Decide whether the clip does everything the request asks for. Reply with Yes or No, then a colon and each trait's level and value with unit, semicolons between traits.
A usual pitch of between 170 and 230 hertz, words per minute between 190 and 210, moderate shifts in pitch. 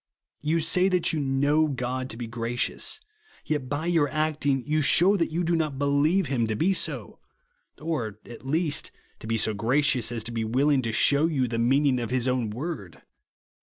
No: medium, 140 Hz; average, 200 wpm; average, 4.6 semitones